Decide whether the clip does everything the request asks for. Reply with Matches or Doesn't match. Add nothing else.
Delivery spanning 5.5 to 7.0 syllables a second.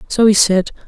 Doesn't match